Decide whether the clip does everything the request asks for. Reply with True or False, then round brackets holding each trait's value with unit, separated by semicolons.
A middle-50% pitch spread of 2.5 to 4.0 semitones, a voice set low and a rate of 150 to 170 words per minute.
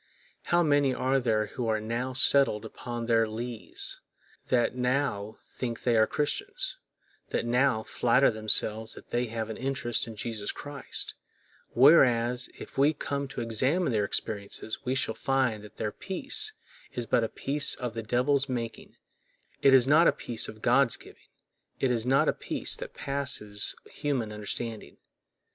True (3.6 semitones; 125 Hz; 155 wpm)